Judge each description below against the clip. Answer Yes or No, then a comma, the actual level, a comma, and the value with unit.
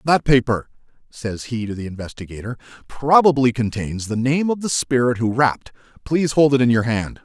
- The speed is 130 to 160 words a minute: No, average, 180 wpm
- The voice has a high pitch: No, low, 125 Hz